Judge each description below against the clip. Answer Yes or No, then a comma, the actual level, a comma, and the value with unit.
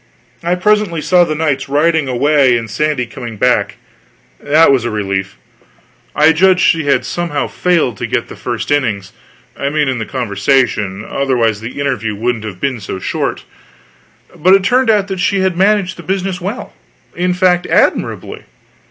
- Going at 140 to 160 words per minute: No, average, 170 wpm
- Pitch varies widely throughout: Yes, wide, 7.3 semitones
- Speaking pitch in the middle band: Yes, medium, 145 Hz